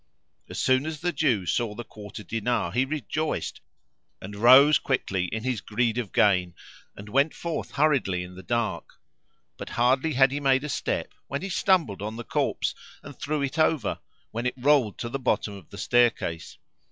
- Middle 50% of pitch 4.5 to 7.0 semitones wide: Yes, average, 5.2 semitones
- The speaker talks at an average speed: Yes, average, 185 wpm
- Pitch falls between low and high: No, low, 120 Hz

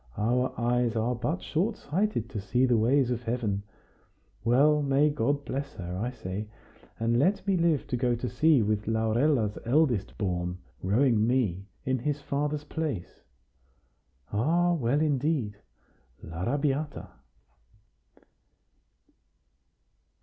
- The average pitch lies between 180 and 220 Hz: No, low, 125 Hz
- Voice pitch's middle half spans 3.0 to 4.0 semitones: No, average, 4.9 semitones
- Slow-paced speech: Yes, slow, 120 wpm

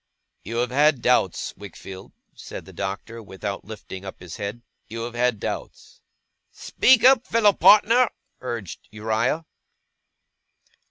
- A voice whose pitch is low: Yes, low, 115 Hz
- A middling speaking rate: No, slow, 125 wpm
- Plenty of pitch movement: Yes, wide, 7.0 semitones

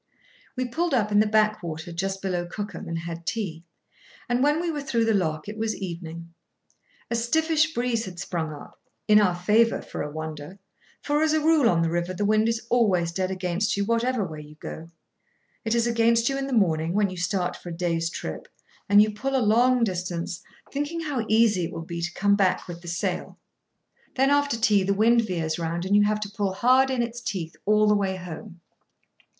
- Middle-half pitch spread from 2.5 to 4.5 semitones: No, average, 5.2 semitones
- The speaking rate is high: Yes, fast, 210 wpm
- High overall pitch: Yes, high, 205 Hz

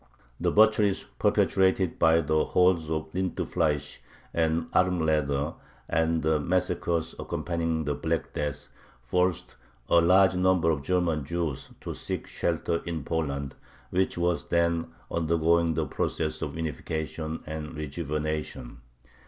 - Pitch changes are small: Yes, narrow, 2.0 semitones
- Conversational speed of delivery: No, slow, 120 wpm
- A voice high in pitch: No, very low, 80 Hz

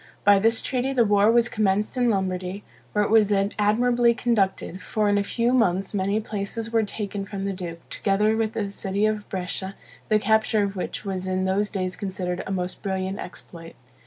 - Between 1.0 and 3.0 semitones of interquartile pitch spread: Yes, narrow, 2.4 semitones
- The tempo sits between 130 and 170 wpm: No, average, 190 wpm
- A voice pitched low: No, high, 205 Hz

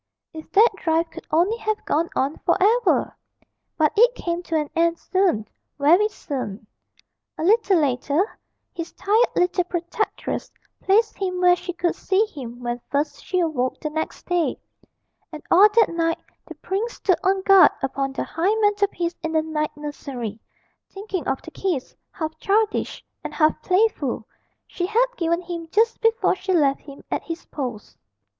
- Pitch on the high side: Yes, very high, 345 Hz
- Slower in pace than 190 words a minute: Yes, average, 165 wpm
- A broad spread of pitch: No, average, 4.4 semitones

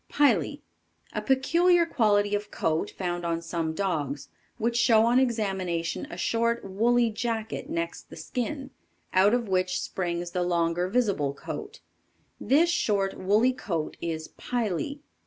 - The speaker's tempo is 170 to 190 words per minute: No, average, 140 wpm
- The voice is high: Yes, high, 205 Hz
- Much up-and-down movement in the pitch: Yes, wide, 5.8 semitones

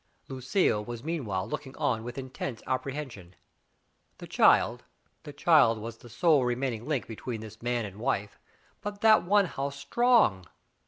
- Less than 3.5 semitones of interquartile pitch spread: No, average, 4.9 semitones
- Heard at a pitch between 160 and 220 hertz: No, low, 130 Hz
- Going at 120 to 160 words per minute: Yes, average, 155 wpm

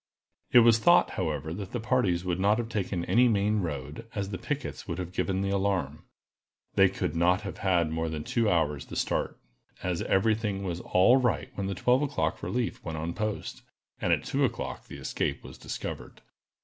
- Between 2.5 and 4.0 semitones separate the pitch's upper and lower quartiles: No, average, 4.5 semitones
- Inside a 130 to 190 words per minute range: No, average, 200 wpm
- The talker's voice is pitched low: Yes, very low, 95 Hz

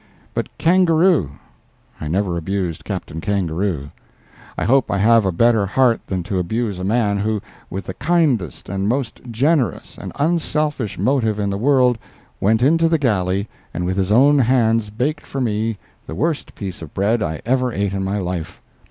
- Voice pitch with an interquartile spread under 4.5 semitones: No, wide, 5.5 semitones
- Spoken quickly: No, average, 170 wpm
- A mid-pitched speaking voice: No, low, 110 Hz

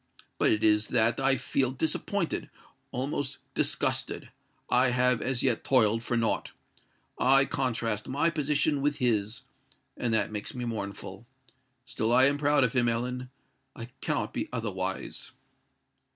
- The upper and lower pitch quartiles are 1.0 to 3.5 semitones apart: Yes, average, 3.0 semitones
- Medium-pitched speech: No, low, 125 Hz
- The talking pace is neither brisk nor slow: No, slow, 125 wpm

